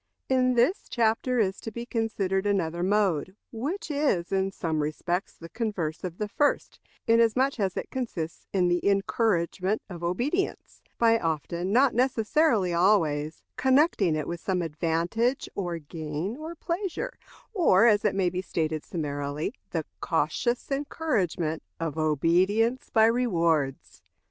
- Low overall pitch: No, high, 195 Hz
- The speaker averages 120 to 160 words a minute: Yes, average, 140 wpm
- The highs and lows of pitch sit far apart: Yes, wide, 6.0 semitones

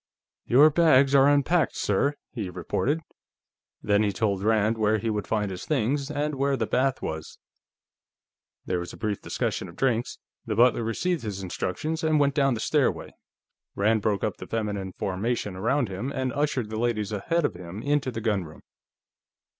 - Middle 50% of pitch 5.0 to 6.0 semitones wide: Yes, wide, 5.4 semitones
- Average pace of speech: Yes, average, 175 wpm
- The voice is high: No, low, 115 Hz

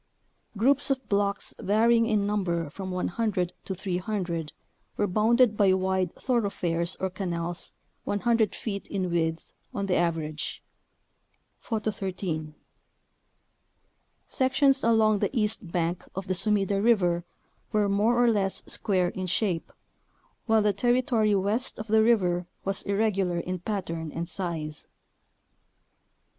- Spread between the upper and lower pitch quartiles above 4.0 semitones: No, average, 3.6 semitones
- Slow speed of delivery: Yes, slow, 125 wpm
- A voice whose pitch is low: No, high, 195 Hz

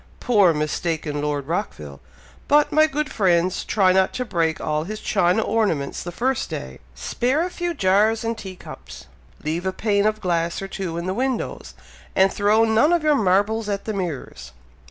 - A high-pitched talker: Yes, high, 195 Hz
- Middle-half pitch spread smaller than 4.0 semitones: No, average, 4.8 semitones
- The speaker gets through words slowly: No, average, 180 wpm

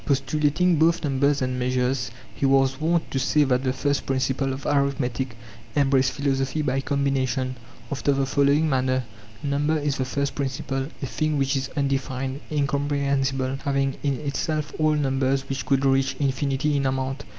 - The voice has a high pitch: No, low, 135 Hz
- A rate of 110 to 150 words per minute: No, average, 170 wpm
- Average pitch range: No, narrow, 1.3 semitones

